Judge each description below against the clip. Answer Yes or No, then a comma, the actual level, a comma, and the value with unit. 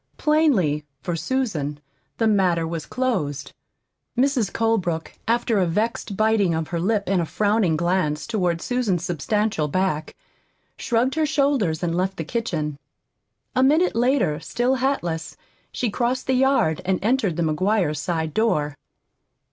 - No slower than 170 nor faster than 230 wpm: No, average, 140 wpm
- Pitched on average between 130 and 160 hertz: No, high, 195 Hz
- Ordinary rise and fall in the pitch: No, wide, 6.8 semitones